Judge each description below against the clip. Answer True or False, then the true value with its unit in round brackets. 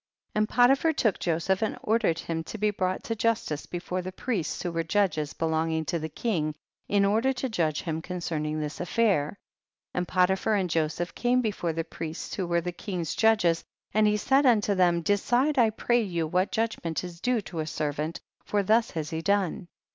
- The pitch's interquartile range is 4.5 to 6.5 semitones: True (4.9 semitones)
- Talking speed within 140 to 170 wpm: False (200 wpm)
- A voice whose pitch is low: False (185 Hz)